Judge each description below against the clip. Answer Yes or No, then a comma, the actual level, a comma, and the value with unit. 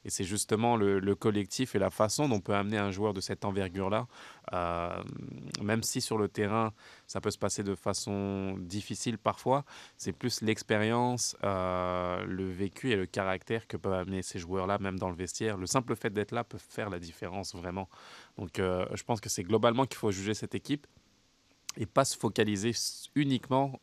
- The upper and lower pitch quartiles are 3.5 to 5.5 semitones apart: No, average, 2.9 semitones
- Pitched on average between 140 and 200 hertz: No, low, 105 Hz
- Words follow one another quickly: No, average, 195 wpm